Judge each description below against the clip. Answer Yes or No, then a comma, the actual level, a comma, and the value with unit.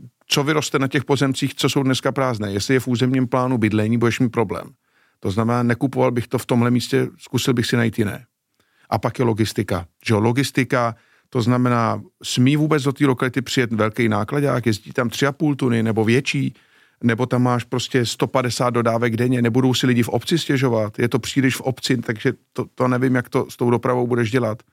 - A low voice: Yes, low, 125 Hz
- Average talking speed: No, fast, 200 wpm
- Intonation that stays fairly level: Yes, narrow, 2.2 semitones